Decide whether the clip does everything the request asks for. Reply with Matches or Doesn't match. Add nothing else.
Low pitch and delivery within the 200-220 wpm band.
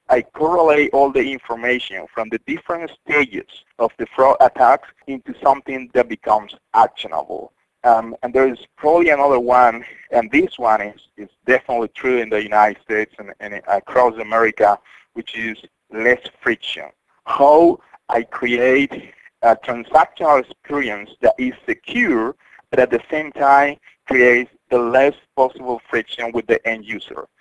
Doesn't match